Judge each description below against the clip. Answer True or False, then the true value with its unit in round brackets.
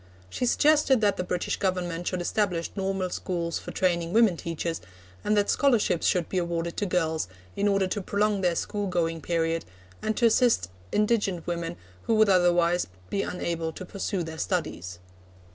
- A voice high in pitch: False (180 Hz)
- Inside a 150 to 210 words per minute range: True (170 wpm)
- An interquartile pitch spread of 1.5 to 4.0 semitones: True (3.3 semitones)